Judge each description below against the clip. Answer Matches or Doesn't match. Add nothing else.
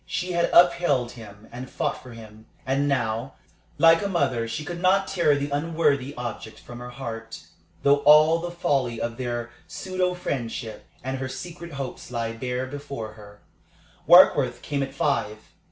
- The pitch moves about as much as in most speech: Doesn't match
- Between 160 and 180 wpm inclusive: Matches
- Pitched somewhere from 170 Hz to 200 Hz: Doesn't match